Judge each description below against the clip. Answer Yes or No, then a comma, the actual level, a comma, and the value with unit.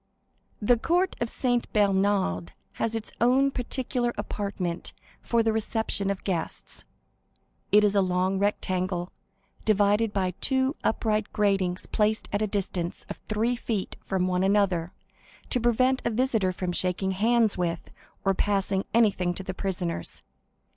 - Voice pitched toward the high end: Yes, high, 205 Hz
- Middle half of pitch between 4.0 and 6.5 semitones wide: No, average, 3.5 semitones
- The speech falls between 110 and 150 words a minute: Yes, average, 140 wpm